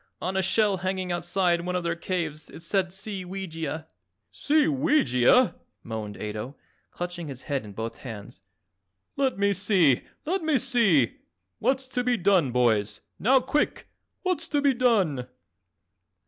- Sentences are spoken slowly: No, average, 145 wpm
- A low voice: No, medium, 185 Hz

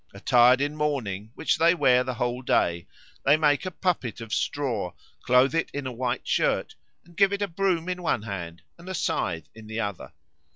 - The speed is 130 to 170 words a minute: No, average, 200 wpm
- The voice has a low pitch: Yes, low, 130 Hz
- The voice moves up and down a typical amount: No, wide, 6.6 semitones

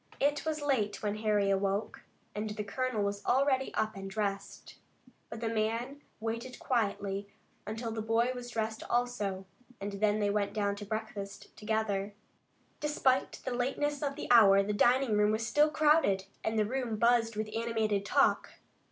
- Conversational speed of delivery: Yes, average, 160 wpm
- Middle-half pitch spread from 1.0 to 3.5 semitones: Yes, average, 3.2 semitones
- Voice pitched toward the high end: Yes, high, 220 Hz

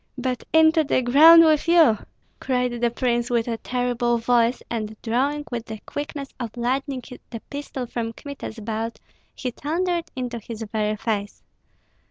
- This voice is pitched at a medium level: No, high, 245 Hz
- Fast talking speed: No, average, 155 wpm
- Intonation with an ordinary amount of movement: Yes, average, 3.6 semitones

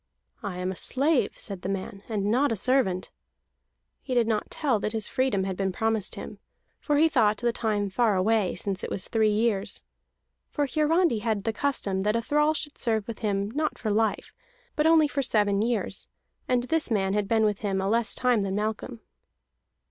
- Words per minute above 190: Yes, average, 200 wpm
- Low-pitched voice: No, high, 220 Hz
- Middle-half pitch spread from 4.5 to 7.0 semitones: No, average, 4.1 semitones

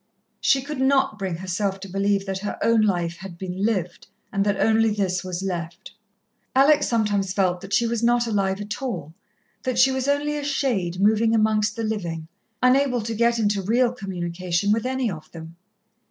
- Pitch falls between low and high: No, high, 210 Hz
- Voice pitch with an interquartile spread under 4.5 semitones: Yes, average, 4.0 semitones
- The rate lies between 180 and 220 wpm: Yes, average, 185 wpm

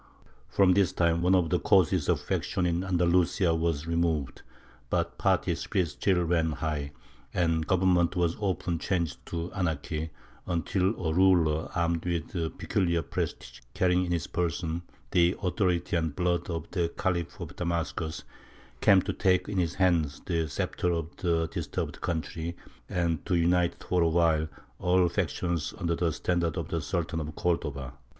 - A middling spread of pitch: No, narrow, 1.7 semitones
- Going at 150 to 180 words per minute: Yes, average, 155 wpm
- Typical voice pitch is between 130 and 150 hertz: No, very low, 85 Hz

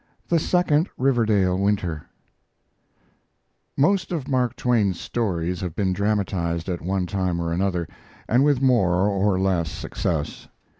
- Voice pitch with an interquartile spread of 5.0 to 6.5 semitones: Yes, wide, 5.6 semitones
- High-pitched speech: No, low, 100 Hz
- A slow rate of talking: Yes, slow, 130 wpm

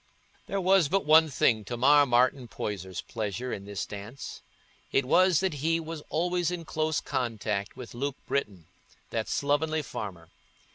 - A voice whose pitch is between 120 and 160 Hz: Yes, medium, 140 Hz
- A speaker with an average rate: Yes, average, 155 wpm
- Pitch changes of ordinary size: No, wide, 6.5 semitones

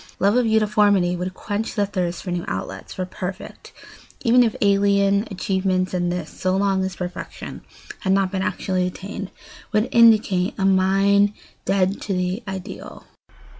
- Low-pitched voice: No, high, 195 Hz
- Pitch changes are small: Yes, narrow, 1.7 semitones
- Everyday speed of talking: Yes, average, 155 wpm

